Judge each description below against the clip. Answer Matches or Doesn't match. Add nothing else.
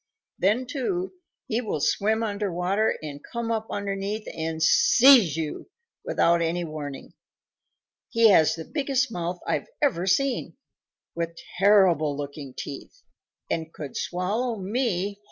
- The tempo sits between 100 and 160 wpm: Matches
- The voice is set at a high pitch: Matches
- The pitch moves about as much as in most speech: Doesn't match